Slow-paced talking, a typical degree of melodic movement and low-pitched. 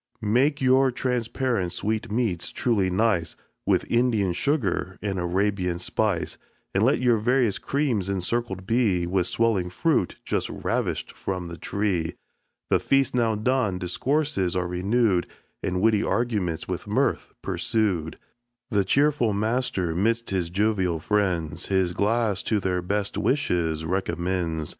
Yes: slow, 130 wpm; average, 4.6 semitones; low, 100 Hz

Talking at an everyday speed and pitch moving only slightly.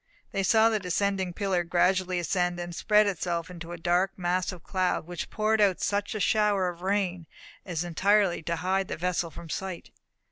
Yes: average, 185 wpm; narrow, 2.3 semitones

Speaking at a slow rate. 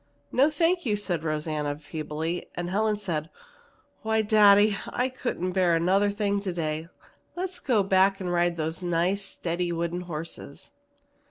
No: average, 145 wpm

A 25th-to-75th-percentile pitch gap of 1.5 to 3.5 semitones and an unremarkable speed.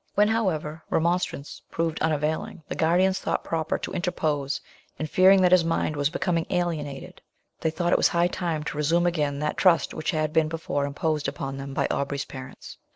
Yes: average, 2.8 semitones; average, 180 wpm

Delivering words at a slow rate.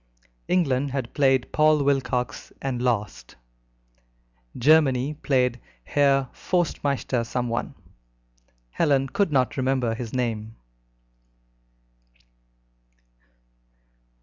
Yes: slow, 75 wpm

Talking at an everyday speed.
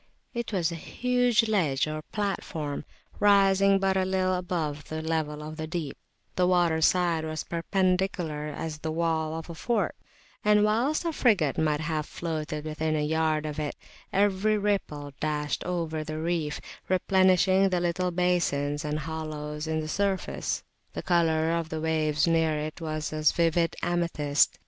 Yes: average, 160 wpm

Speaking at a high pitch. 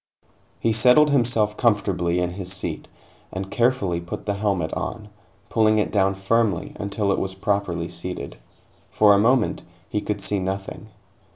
No: low, 100 Hz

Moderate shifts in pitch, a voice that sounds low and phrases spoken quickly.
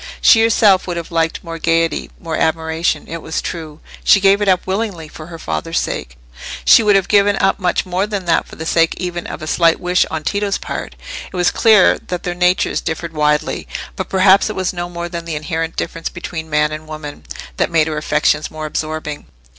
No: average, 3.0 semitones; medium, 170 Hz; fast, 210 wpm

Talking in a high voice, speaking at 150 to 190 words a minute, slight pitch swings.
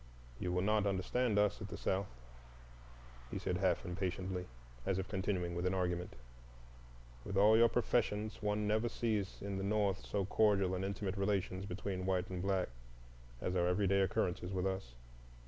No: very low, 95 Hz; average, 165 wpm; narrow, 2.0 semitones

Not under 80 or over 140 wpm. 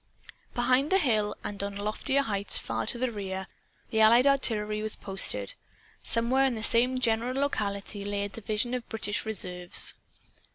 No: average, 160 wpm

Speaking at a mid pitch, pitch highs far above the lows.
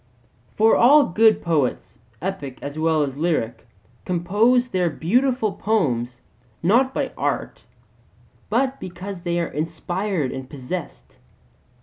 Yes: medium, 175 Hz; wide, 6.9 semitones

